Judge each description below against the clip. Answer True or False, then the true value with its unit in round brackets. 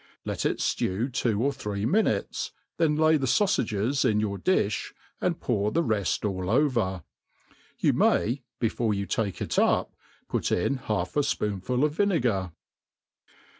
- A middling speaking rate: True (150 wpm)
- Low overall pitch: True (115 Hz)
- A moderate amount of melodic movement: False (6.0 semitones)